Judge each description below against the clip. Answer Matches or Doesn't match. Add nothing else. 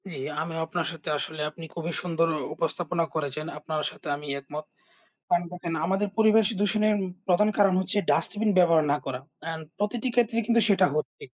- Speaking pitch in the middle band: Matches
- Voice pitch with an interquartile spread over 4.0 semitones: Matches